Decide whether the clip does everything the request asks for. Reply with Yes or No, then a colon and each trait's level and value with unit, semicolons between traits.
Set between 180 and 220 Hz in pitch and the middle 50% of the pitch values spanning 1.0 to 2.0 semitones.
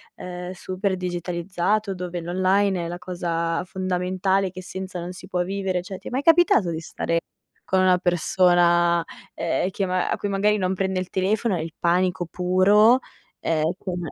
Yes: medium, 185 Hz; narrow, 1.4 semitones